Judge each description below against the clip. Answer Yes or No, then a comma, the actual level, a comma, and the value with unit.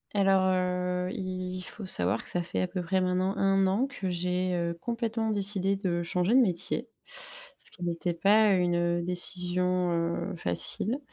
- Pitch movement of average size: No, narrow, 1.8 semitones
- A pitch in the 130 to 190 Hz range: Yes, medium, 185 Hz